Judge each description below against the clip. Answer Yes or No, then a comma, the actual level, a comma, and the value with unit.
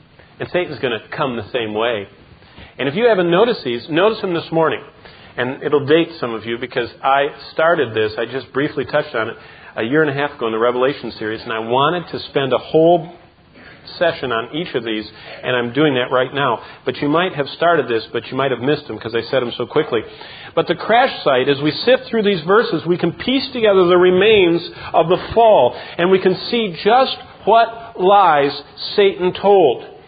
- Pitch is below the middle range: No, medium, 155 Hz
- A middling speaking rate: No, fast, 215 wpm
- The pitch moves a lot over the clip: Yes, wide, 7.0 semitones